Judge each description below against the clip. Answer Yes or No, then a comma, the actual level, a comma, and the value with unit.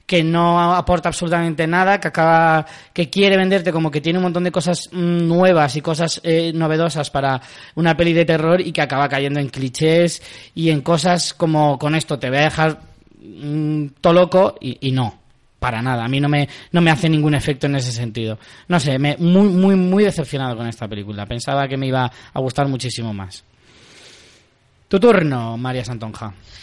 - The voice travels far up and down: No, average, 4.5 semitones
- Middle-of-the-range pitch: Yes, medium, 155 Hz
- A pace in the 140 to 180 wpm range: No, fast, 190 wpm